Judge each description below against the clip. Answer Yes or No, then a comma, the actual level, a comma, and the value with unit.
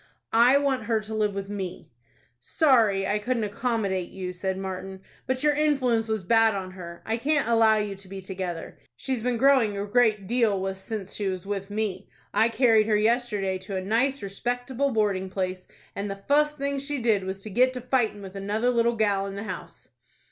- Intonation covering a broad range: No, average, 3.9 semitones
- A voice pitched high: Yes, high, 215 Hz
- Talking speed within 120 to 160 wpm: No, average, 200 wpm